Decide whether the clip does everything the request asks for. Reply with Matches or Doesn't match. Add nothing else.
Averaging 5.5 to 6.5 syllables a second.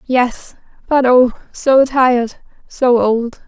Doesn't match